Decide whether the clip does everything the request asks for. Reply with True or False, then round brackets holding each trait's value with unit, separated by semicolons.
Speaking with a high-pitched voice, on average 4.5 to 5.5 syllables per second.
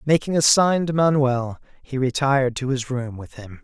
False (135 Hz; 5.1 syllables/s)